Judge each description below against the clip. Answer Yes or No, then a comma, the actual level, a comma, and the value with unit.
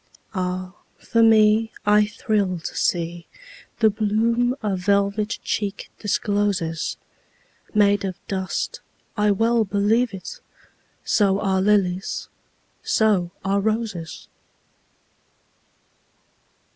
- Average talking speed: No, slow, 80 wpm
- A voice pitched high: Yes, high, 205 Hz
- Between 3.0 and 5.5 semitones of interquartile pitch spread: No, narrow, 2.5 semitones